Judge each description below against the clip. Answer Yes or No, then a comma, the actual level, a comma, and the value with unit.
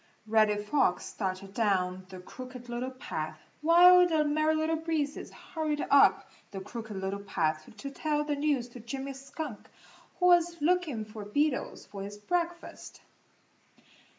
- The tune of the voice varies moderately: No, wide, 7.1 semitones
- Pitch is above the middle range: Yes, very high, 265 Hz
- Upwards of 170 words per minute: No, average, 145 wpm